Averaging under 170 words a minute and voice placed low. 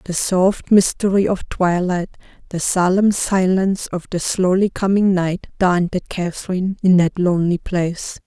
No: average, 140 wpm; medium, 185 Hz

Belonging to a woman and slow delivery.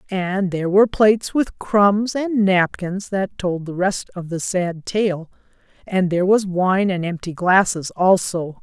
No: female; average, 160 wpm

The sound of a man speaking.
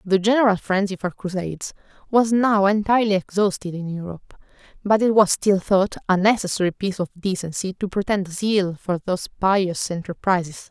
No: female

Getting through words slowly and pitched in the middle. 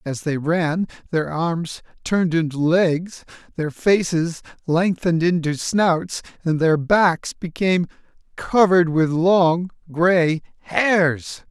Yes: slow, 115 wpm; medium, 170 Hz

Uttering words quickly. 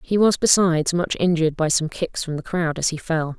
Yes: fast, 250 wpm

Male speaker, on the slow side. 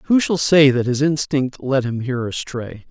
No: male; fast, 205 wpm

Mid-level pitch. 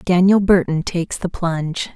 Yes: medium, 175 Hz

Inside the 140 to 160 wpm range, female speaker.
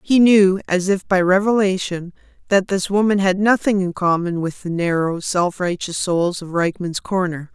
No: average, 175 wpm; female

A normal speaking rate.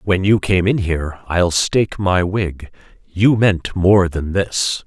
Yes: average, 175 wpm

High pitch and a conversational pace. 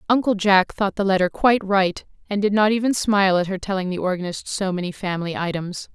No: high, 195 Hz; fast, 210 wpm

